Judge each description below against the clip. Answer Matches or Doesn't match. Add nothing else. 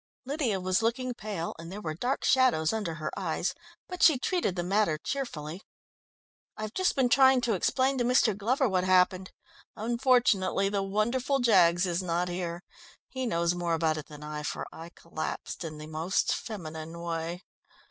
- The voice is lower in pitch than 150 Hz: Doesn't match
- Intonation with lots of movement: Matches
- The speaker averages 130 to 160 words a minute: Doesn't match